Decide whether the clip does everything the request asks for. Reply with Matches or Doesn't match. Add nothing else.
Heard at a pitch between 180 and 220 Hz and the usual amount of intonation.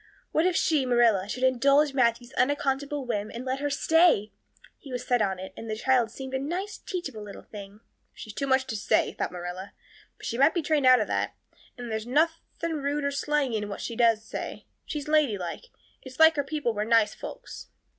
Doesn't match